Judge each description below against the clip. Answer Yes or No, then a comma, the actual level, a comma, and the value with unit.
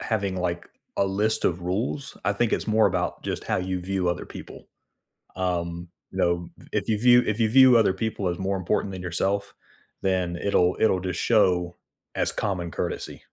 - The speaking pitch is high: No, very low, 95 Hz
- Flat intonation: No, average, 3.3 semitones